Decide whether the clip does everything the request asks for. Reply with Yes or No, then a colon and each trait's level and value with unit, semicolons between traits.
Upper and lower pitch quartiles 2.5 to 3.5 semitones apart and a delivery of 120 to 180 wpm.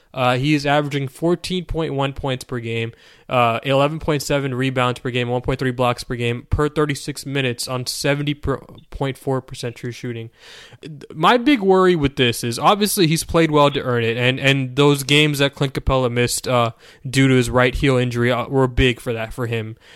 No: average, 2.8 semitones; fast, 205 wpm